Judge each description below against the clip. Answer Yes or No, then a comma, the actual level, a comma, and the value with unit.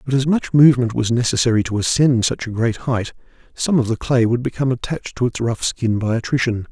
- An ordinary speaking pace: No, fast, 225 wpm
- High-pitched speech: No, low, 120 Hz